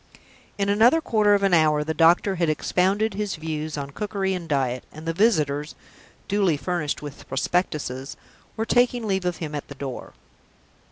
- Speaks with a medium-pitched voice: Yes, medium, 170 Hz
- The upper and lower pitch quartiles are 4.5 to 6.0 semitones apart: Yes, average, 5.2 semitones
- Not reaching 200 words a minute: Yes, average, 170 wpm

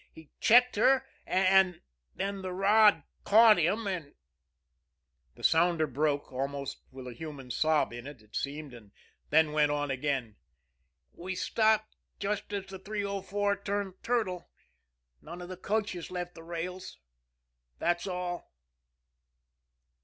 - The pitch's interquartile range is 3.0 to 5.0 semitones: No, wide, 5.6 semitones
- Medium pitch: Yes, medium, 175 Hz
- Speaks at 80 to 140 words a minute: Yes, slow, 135 wpm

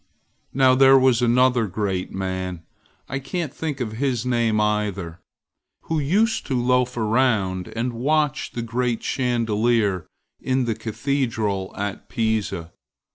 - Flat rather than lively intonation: No, average, 3.8 semitones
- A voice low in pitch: Yes, low, 120 Hz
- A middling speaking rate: No, slow, 130 wpm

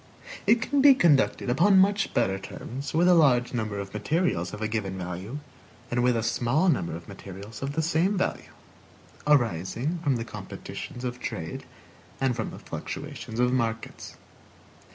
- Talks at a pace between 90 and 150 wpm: No, average, 165 wpm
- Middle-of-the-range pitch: No, low, 125 Hz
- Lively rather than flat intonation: Yes, wide, 6.8 semitones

